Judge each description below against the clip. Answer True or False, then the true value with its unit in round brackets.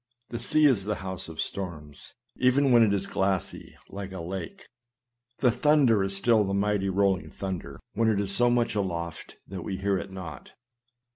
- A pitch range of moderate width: True (3.5 semitones)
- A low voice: True (100 Hz)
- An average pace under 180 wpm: False (185 wpm)